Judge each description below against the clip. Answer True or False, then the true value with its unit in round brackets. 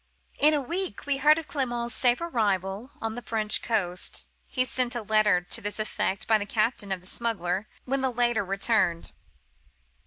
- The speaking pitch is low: False (225 Hz)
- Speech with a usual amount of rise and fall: True (4.1 semitones)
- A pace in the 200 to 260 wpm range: False (180 wpm)